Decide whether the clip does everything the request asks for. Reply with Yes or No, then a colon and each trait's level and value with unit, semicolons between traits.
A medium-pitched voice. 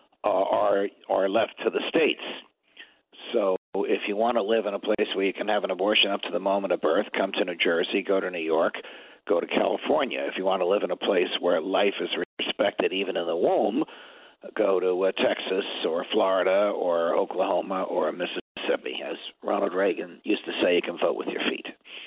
No: low, 100 Hz